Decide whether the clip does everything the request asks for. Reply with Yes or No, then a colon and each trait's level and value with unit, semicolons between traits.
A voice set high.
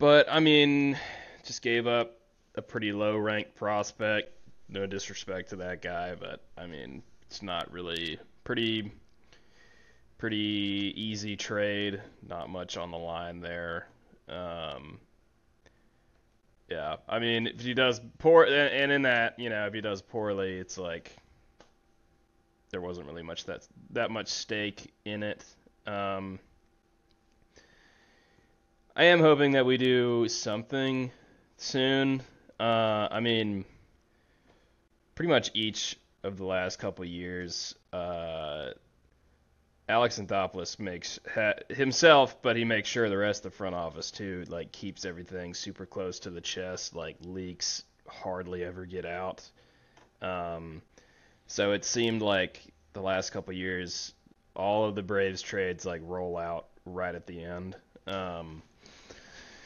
No: low, 100 Hz